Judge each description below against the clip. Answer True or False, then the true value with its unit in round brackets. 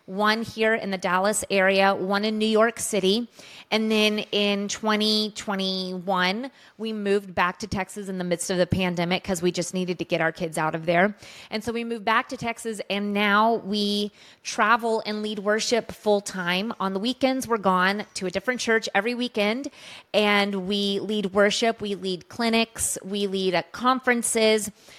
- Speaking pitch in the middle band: False (205 Hz)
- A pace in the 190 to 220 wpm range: False (180 wpm)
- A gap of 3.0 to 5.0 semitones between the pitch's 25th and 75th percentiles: False (2.6 semitones)